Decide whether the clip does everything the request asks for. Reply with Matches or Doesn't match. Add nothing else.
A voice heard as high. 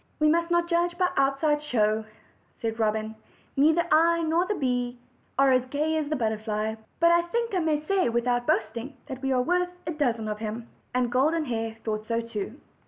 Matches